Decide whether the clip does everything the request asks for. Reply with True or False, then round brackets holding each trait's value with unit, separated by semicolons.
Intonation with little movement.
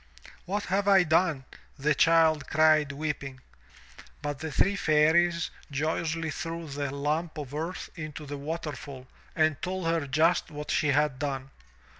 True (2.3 semitones)